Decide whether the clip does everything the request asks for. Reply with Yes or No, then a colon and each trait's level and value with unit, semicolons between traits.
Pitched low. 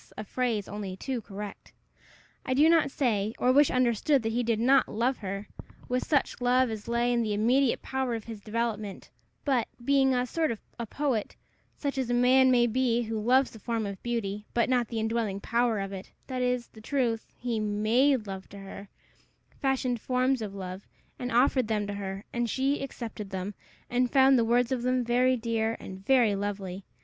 No: high, 235 Hz